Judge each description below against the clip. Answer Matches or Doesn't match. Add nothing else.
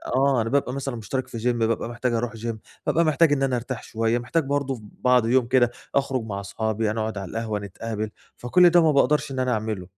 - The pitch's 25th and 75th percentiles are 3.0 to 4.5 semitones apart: Matches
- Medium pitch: Doesn't match